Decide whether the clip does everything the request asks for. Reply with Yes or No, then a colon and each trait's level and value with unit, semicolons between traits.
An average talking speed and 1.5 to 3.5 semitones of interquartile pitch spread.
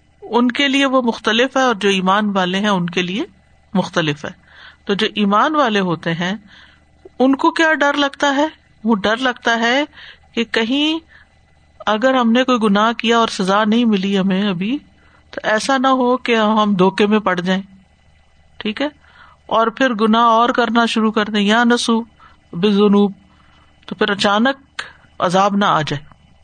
No: average, 175 wpm; average, 4.2 semitones